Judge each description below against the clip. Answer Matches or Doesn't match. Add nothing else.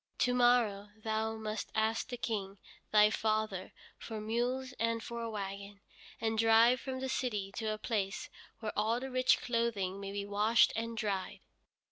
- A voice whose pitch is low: Doesn't match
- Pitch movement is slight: Matches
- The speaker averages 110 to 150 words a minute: Doesn't match